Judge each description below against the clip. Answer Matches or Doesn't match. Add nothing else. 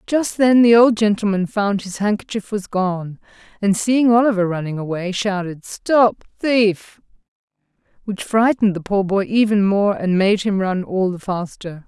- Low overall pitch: Doesn't match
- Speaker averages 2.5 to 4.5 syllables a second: Matches